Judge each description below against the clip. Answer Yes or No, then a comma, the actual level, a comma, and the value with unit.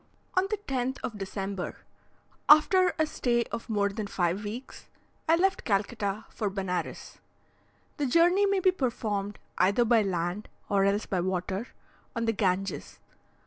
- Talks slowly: No, average, 145 wpm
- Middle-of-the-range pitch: No, high, 215 Hz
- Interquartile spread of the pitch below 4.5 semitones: No, wide, 5.4 semitones